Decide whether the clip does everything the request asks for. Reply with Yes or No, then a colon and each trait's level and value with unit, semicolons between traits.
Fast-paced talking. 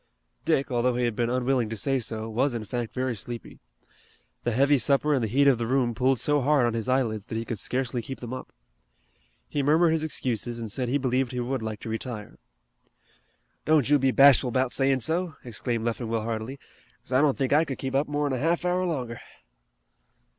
Yes: fast, 210 wpm